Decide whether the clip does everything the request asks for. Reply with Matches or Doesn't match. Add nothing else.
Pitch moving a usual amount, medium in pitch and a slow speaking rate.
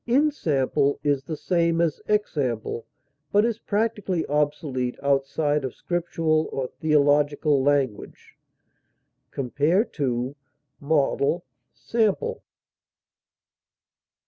Matches